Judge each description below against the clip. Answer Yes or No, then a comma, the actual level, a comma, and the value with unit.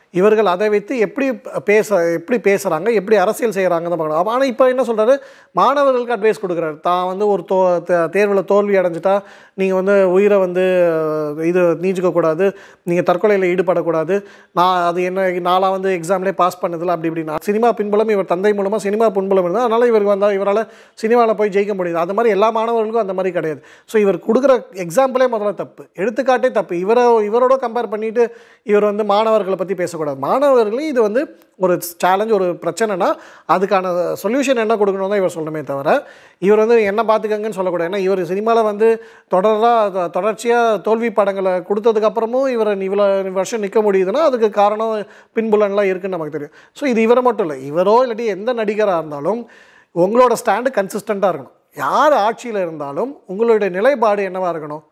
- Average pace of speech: No, fast, 160 wpm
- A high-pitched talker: Yes, high, 205 Hz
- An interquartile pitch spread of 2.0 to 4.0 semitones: Yes, average, 3.7 semitones